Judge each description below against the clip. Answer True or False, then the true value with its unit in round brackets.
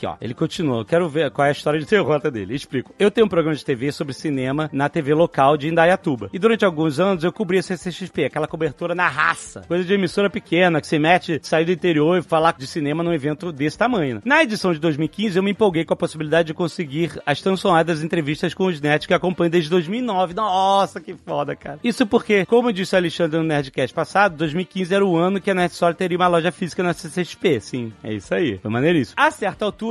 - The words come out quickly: True (235 wpm)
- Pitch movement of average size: True (3.5 semitones)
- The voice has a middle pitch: True (175 Hz)